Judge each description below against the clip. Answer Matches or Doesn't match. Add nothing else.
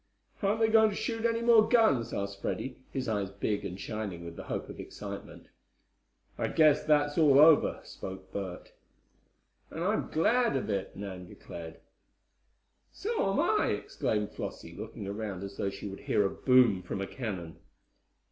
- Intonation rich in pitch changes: Matches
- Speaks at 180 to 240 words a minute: Doesn't match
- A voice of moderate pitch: Doesn't match